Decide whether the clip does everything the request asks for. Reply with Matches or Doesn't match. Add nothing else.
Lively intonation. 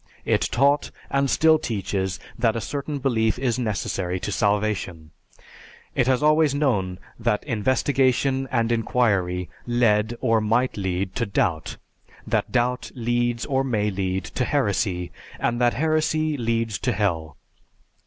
Doesn't match